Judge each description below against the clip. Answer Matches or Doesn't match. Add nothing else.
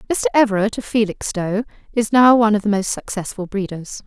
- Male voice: Doesn't match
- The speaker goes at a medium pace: Matches